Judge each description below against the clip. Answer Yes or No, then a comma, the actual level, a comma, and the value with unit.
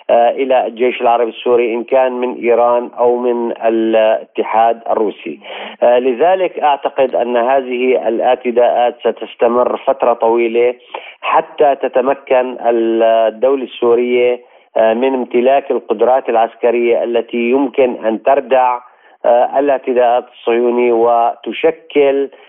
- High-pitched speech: No, low, 120 Hz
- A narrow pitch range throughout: Yes, narrow, 1.7 semitones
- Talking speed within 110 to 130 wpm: No, average, 95 wpm